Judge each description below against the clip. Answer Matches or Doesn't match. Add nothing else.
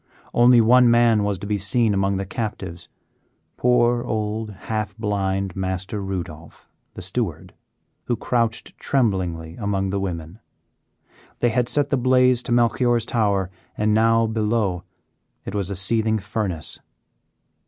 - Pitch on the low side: Matches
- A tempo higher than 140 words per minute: Doesn't match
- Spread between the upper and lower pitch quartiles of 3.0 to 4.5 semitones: Matches